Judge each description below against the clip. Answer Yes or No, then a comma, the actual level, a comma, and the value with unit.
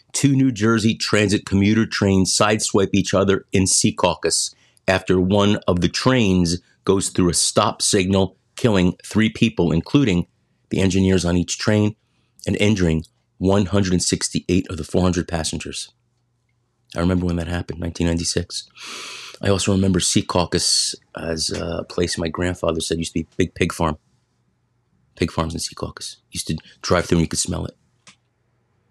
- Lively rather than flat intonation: No, average, 3.8 semitones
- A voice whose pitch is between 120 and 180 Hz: No, very low, 95 Hz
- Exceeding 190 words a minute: No, average, 155 wpm